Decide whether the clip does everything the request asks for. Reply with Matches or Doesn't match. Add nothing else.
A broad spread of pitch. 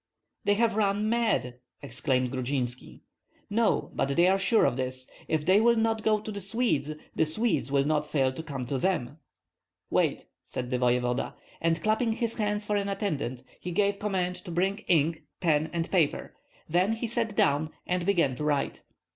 Matches